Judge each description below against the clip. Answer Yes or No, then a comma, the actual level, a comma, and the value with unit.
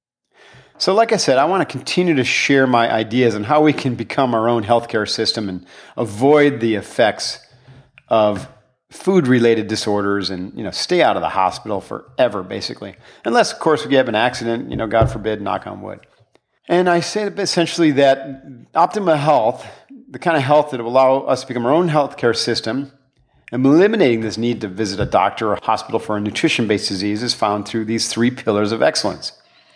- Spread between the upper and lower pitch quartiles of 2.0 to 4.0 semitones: No, average, 4.5 semitones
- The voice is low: Yes, low, 125 Hz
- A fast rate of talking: No, average, 190 wpm